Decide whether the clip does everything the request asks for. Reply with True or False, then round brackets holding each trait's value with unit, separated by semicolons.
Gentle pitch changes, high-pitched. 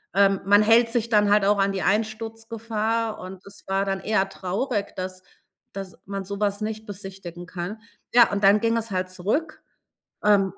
True (2.3 semitones; 205 Hz)